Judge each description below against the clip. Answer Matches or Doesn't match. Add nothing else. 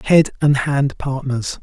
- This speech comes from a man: Matches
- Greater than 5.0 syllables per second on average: Doesn't match